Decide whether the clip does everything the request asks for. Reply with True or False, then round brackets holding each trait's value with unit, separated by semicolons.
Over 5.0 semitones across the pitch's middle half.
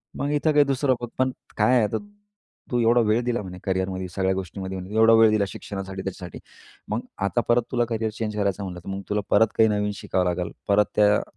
False (3.7 semitones)